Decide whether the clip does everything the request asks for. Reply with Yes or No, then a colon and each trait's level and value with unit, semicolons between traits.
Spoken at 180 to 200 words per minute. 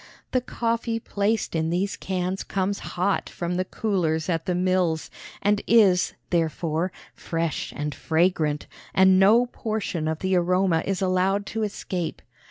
No: average, 145 wpm